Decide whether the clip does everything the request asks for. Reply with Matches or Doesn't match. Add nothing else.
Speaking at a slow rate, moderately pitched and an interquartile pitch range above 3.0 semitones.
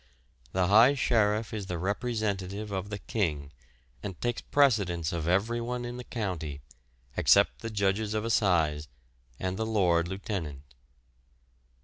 Doesn't match